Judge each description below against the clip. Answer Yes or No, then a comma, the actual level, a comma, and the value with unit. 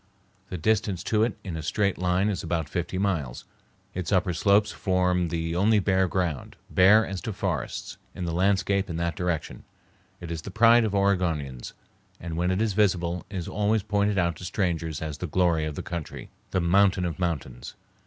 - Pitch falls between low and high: No, very low, 90 Hz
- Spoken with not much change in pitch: No, average, 3.0 semitones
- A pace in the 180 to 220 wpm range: Yes, average, 190 wpm